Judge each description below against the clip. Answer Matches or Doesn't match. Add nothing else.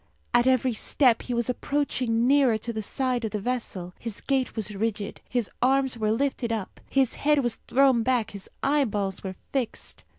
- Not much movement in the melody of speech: Doesn't match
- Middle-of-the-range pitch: Doesn't match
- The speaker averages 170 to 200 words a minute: Matches